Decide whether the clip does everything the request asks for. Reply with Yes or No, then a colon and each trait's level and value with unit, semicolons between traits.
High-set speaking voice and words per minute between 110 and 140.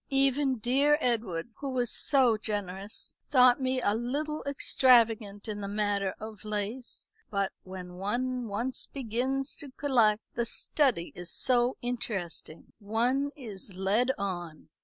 Yes: high, 230 Hz; slow, 135 wpm